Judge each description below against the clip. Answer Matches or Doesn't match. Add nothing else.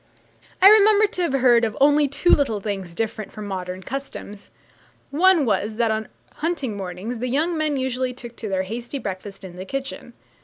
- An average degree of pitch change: Doesn't match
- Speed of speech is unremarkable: Matches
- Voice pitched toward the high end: Matches